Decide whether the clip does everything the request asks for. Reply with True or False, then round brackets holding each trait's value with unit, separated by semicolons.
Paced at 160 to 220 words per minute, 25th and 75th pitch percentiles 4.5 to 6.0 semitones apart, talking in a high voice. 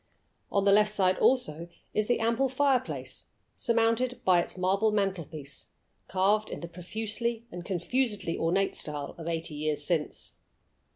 False (140 wpm; 5.2 semitones; 195 Hz)